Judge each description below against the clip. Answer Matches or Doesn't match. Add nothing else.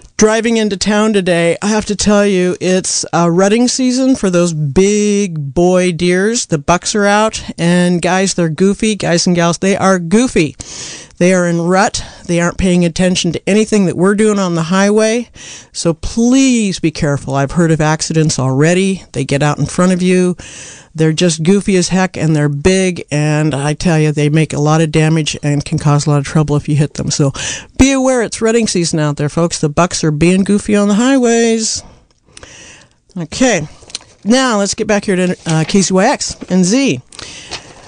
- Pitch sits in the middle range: Matches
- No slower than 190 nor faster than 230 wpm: Matches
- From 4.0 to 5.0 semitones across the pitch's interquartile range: Matches